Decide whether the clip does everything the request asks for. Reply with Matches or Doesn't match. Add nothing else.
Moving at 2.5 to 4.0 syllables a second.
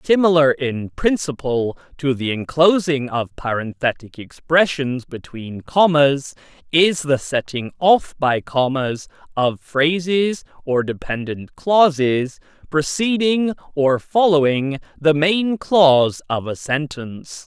Matches